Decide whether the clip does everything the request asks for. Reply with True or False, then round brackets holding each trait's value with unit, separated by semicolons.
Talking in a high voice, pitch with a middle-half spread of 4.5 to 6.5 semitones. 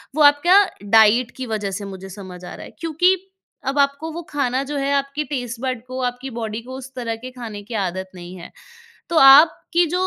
True (255 Hz; 4.8 semitones)